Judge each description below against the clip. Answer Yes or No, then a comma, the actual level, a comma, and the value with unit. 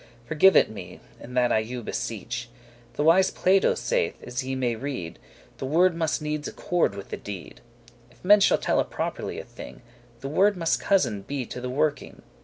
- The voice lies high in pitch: No, low, 135 Hz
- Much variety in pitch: Yes, wide, 6.0 semitones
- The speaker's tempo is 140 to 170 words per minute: No, average, 190 wpm